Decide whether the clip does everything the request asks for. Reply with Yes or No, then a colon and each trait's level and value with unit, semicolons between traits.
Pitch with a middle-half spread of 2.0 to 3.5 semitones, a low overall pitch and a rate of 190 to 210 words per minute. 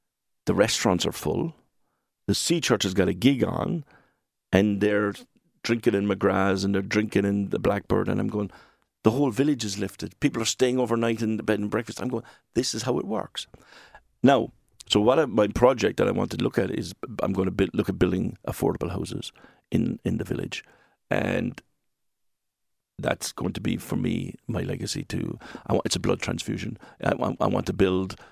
Yes: average, 3.2 semitones; low, 105 Hz; average, 200 wpm